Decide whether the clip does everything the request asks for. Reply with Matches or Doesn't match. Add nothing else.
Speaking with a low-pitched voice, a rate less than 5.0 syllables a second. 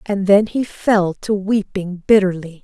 Doesn't match